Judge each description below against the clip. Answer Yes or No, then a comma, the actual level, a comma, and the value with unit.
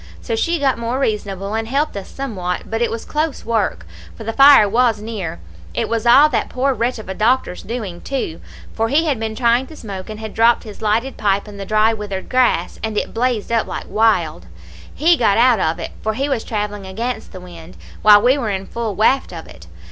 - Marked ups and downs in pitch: No, average, 3.6 semitones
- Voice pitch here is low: No, high, 225 Hz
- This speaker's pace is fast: Yes, fast, 225 wpm